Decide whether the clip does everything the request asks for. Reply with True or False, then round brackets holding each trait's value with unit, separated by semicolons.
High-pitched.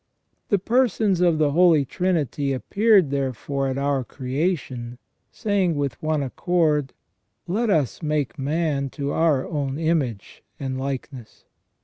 False (145 Hz)